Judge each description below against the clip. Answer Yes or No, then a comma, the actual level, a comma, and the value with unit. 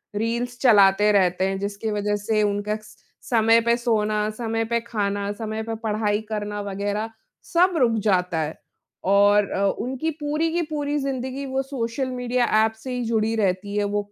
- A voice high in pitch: Yes, high, 220 Hz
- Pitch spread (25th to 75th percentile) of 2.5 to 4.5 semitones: Yes, average, 3.1 semitones